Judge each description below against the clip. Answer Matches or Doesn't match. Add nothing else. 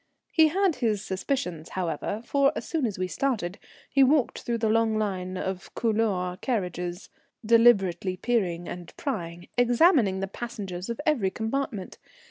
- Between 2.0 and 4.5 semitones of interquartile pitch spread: Doesn't match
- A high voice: Matches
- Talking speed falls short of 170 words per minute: Matches